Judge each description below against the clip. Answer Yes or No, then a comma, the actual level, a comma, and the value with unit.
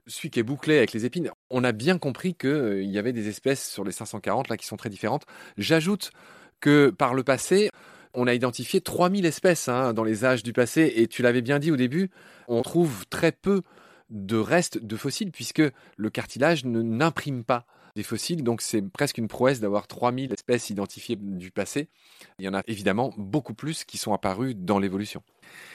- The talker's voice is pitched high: No, low, 125 Hz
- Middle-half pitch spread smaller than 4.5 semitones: No, average, 5.0 semitones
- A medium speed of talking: Yes, average, 200 wpm